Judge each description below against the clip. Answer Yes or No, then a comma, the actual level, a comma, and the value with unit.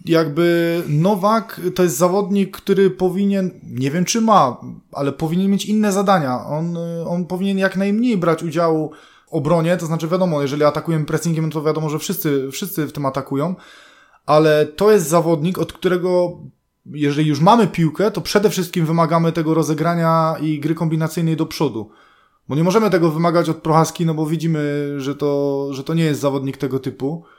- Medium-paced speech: No, fast, 175 wpm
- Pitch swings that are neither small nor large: Yes, average, 3.2 semitones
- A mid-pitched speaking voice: Yes, medium, 165 Hz